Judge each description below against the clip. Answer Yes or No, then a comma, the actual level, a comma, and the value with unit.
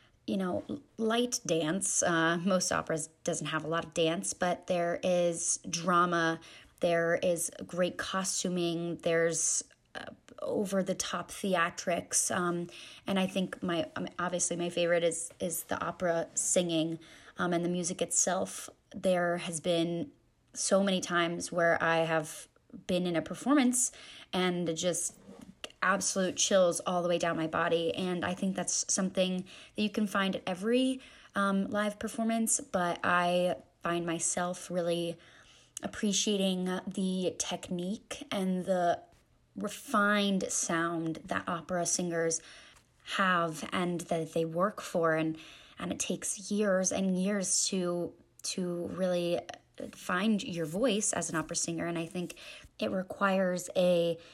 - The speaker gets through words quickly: No, average, 140 wpm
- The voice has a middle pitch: Yes, medium, 175 Hz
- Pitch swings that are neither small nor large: No, narrow, 2.2 semitones